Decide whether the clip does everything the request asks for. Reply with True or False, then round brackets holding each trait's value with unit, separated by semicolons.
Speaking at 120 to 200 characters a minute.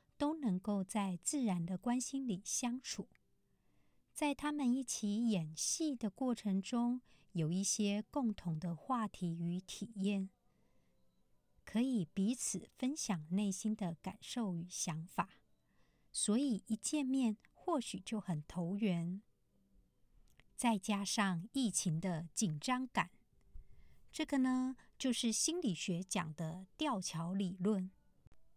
True (170 characters per minute)